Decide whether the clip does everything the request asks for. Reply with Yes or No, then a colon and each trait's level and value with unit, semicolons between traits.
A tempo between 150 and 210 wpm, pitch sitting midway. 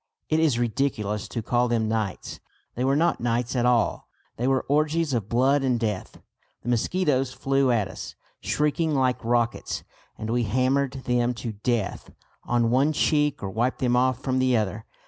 No: average, 175 wpm; low, 125 Hz